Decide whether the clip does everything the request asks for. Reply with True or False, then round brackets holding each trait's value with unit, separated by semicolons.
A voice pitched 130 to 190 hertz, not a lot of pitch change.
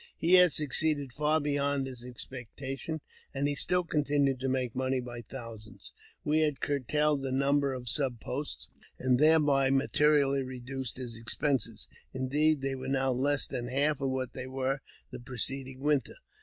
True (135 Hz; 2.1 semitones)